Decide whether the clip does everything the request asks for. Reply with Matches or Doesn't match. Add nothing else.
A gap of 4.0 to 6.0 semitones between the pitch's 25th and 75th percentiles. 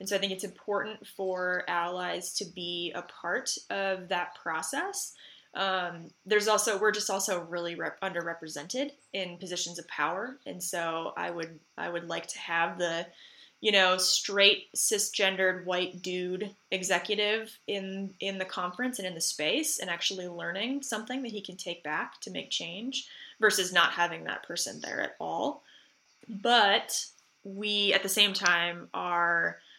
Doesn't match